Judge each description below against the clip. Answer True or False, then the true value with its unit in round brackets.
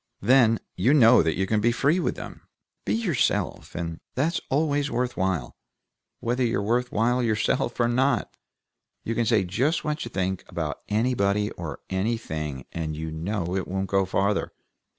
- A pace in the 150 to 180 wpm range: True (170 wpm)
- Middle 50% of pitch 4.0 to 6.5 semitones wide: True (4.9 semitones)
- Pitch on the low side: True (110 Hz)